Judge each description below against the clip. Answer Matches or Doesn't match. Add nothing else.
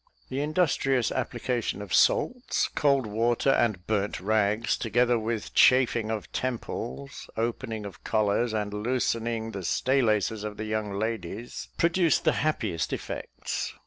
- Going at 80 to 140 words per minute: Matches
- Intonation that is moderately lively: Matches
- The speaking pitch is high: Doesn't match